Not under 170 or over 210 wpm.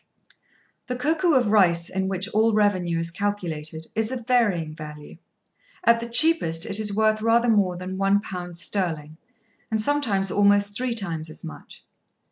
No: average, 160 wpm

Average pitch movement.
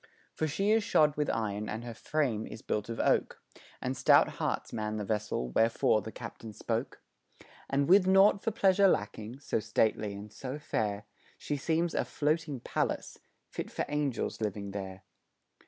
No: wide, 6.4 semitones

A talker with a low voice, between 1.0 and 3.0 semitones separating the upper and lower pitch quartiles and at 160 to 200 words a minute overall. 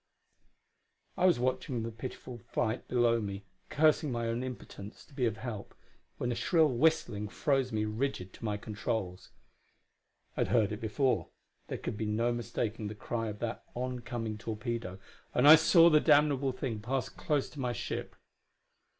No: low, 120 Hz; average, 3.5 semitones; average, 165 wpm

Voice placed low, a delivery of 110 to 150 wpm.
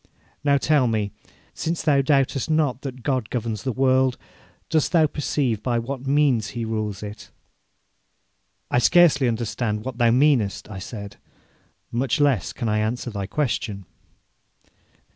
Yes: low, 125 Hz; average, 145 wpm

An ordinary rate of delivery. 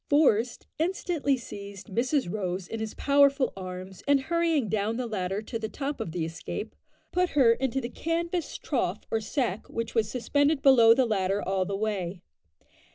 Yes: average, 170 wpm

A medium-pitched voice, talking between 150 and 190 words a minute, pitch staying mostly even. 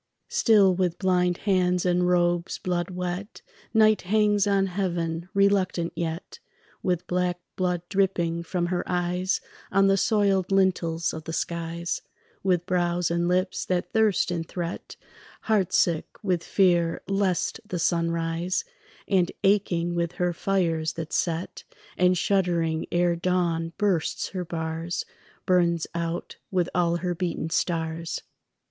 No: medium, 180 Hz; slow, 135 wpm; narrow, 1.9 semitones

